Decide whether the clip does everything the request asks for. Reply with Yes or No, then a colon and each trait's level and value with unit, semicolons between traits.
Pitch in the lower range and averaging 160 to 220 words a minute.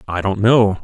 Yes: low, 105 Hz; fast, 215 wpm